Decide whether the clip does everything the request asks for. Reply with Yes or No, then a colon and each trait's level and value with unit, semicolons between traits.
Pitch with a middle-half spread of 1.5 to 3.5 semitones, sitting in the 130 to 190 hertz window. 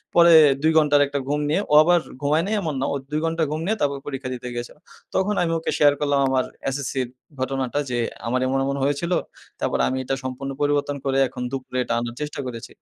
Yes: average, 2.8 semitones; medium, 140 Hz